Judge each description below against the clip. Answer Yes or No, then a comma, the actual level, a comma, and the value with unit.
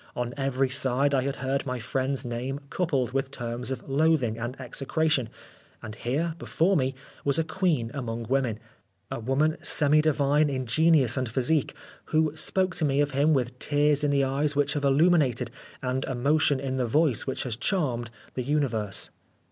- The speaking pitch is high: No, low, 135 Hz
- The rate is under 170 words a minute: No, average, 175 wpm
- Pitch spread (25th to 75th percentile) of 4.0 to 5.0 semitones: No, average, 3.0 semitones